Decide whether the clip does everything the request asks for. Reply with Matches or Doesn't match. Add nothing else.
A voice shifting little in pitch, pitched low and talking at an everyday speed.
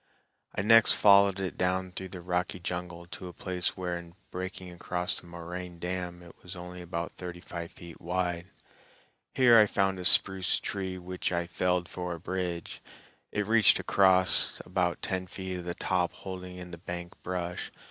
Matches